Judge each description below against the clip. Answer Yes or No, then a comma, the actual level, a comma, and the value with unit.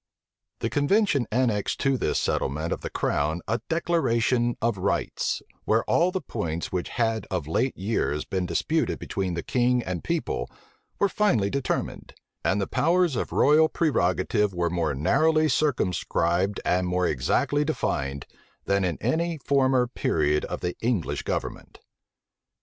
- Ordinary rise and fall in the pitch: No, wide, 8.5 semitones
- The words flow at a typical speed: Yes, average, 145 wpm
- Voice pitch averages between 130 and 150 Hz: No, low, 110 Hz